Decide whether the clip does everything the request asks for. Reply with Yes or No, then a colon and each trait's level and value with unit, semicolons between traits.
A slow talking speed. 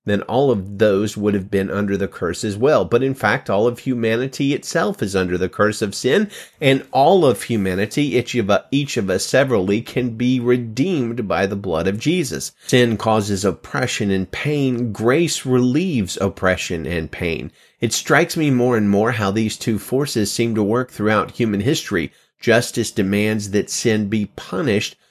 No: average, 180 wpm